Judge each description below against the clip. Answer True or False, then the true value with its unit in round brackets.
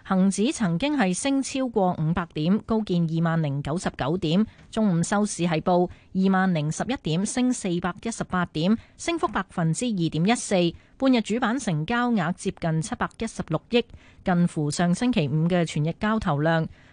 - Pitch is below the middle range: False (185 Hz)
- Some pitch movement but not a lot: True (5.0 semitones)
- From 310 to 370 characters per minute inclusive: False (265 characters per minute)